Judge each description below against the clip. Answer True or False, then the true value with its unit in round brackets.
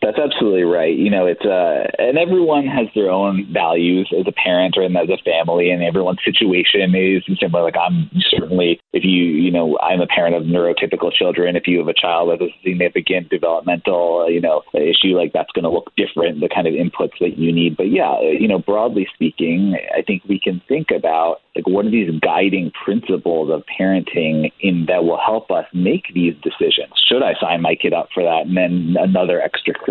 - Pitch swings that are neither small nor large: False (1.9 semitones)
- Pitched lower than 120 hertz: True (90 Hz)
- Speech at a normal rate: False (210 wpm)